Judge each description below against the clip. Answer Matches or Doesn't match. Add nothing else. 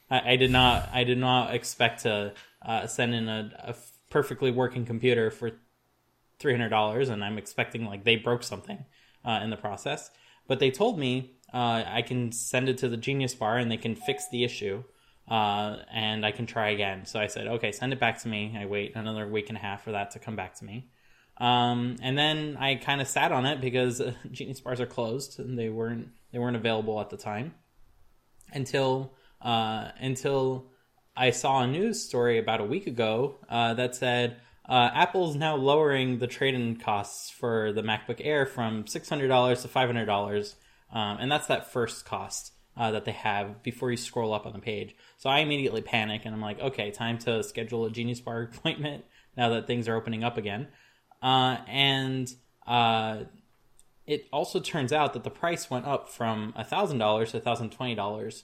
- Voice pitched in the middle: Doesn't match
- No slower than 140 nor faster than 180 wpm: Doesn't match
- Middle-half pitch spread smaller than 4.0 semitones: Matches